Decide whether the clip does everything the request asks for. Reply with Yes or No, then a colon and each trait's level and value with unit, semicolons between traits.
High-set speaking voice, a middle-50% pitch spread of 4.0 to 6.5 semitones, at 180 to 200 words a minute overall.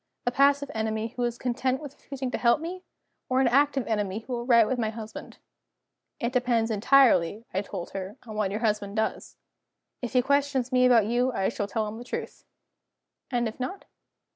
No: high, 240 Hz; average, 3.0 semitones; average, 195 wpm